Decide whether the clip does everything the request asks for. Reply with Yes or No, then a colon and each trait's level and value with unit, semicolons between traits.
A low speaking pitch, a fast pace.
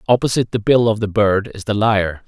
Yes: low, 105 Hz; fast, 240 wpm